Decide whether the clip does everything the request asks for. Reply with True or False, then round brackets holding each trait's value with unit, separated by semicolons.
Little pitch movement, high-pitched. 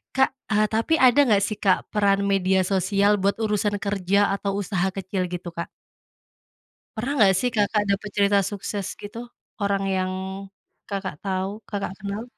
True (1.5 semitones; 200 Hz)